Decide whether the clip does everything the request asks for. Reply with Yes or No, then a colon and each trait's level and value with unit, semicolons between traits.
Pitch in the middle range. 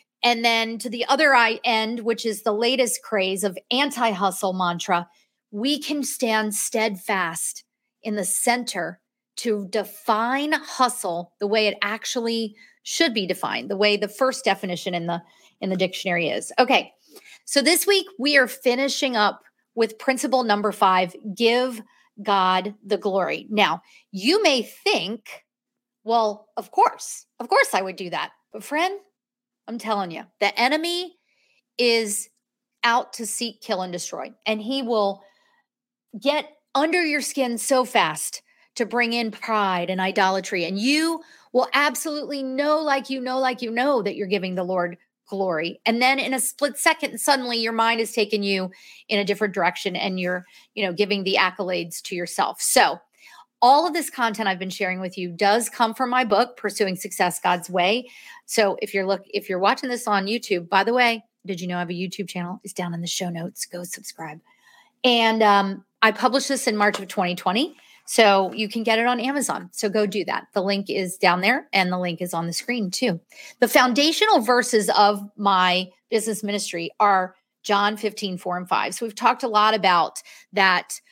No: high, 220 Hz